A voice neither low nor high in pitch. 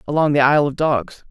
Yes: medium, 145 Hz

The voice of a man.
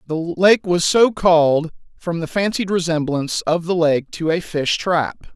Yes: male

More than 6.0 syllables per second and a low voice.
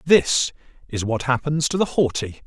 No: 4.6 syllables/s; low, 130 Hz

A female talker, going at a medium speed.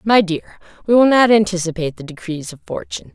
Yes: female; average, 190 wpm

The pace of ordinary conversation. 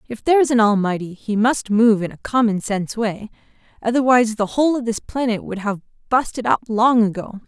Yes: average, 195 wpm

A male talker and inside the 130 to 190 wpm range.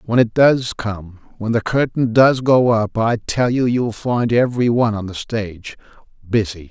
Yes: male; average, 180 wpm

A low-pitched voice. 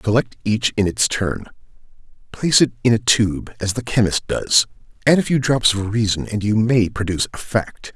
Yes: low, 110 Hz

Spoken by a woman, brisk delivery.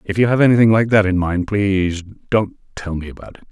No: male; fast, 240 wpm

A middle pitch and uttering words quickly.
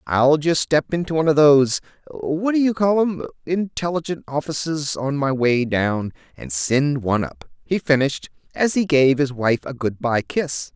No: medium, 145 Hz; average, 175 wpm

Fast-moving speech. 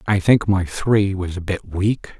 Yes: fast, 220 wpm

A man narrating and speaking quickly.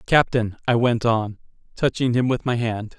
No: male; average, 180 wpm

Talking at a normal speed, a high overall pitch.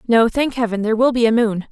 No: fast, 280 wpm; high, 230 Hz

